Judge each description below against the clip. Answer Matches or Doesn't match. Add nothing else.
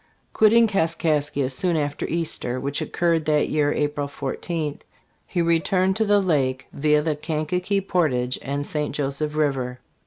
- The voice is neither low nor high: Matches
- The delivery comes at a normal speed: Matches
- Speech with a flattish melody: Doesn't match